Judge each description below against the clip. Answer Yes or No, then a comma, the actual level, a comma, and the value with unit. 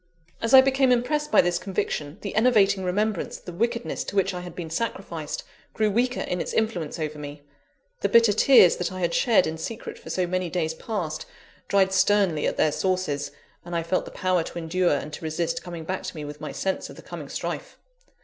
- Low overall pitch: No, medium, 185 Hz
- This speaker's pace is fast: Yes, fast, 215 wpm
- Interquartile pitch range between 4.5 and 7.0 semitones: Yes, average, 4.8 semitones